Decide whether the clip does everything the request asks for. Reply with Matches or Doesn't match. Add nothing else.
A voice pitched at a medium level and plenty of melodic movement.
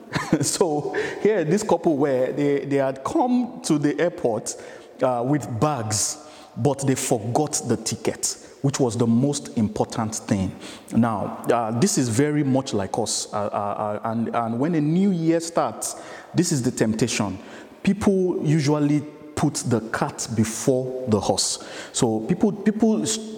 Matches